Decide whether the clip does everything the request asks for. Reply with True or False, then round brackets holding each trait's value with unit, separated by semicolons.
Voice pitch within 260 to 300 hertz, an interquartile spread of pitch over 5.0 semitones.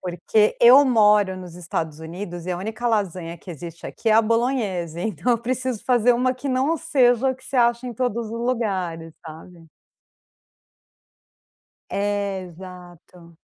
False (205 Hz; 5.5 semitones)